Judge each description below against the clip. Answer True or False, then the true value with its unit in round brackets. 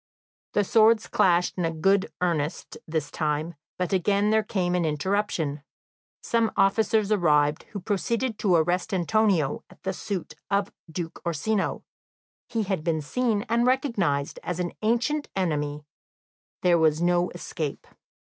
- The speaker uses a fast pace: False (140 wpm)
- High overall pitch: False (180 Hz)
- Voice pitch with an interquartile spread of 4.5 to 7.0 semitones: True (4.8 semitones)